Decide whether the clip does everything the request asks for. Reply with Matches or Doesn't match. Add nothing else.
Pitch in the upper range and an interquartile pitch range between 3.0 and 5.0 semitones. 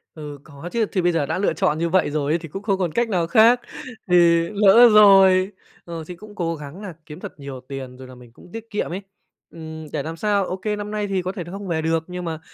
Doesn't match